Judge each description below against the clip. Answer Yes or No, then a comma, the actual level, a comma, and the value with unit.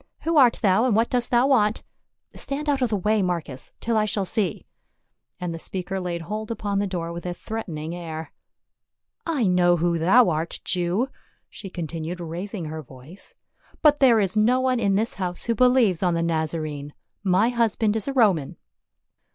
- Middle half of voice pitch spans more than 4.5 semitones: Yes, average, 5.2 semitones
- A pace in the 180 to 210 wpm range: Yes, average, 190 wpm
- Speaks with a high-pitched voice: Yes, high, 195 Hz